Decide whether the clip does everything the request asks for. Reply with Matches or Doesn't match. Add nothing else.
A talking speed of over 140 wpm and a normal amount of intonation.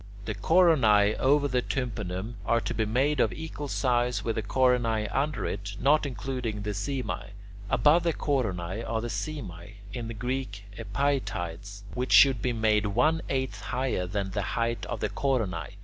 Matches